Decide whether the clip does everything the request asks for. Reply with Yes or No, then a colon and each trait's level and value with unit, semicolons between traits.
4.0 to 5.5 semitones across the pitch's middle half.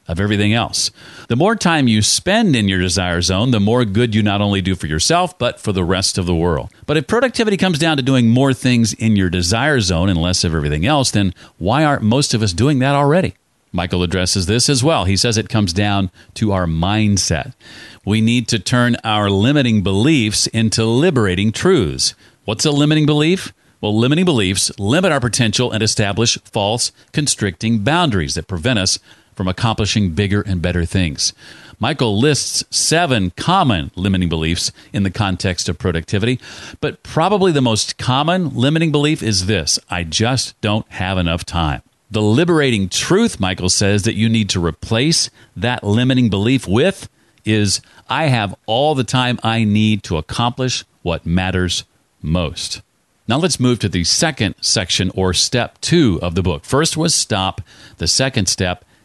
Yes: average, 5.2 semitones